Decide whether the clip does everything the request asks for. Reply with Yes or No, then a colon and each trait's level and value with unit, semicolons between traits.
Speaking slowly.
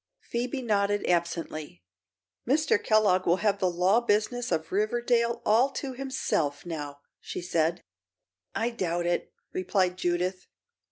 Yes: slow, 125 wpm